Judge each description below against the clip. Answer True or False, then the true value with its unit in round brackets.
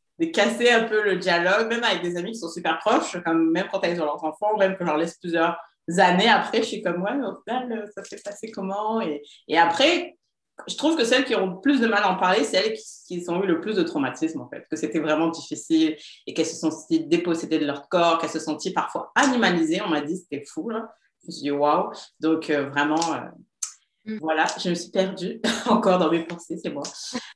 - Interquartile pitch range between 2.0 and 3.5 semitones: False (5.2 semitones)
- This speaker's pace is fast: True (245 wpm)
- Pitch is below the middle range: False (180 Hz)